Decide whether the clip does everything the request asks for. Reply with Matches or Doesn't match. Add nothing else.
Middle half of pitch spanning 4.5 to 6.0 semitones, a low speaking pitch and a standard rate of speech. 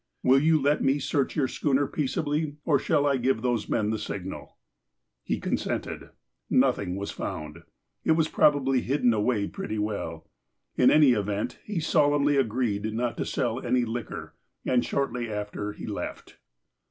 Matches